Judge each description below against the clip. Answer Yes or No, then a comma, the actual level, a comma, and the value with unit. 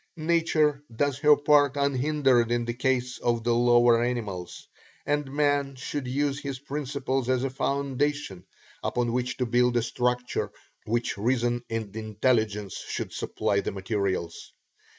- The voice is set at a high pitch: No, low, 125 Hz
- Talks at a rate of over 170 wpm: No, average, 140 wpm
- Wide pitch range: No, average, 3.2 semitones